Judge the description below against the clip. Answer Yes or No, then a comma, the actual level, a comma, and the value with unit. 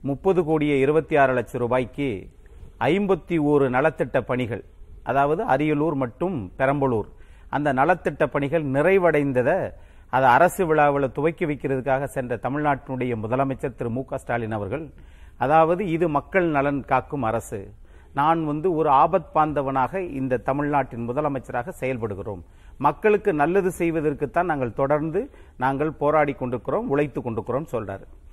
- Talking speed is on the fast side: No, average, 120 wpm